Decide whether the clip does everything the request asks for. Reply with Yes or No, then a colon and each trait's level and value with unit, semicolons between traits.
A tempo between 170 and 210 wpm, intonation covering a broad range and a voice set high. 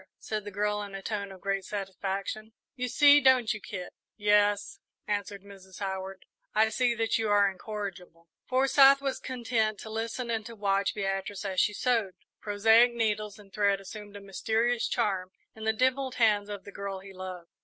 No: average, 180 wpm; narrow, 2.4 semitones; high, 210 Hz